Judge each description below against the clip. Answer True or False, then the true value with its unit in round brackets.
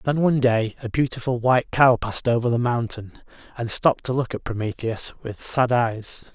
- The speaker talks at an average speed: True (190 wpm)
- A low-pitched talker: True (120 Hz)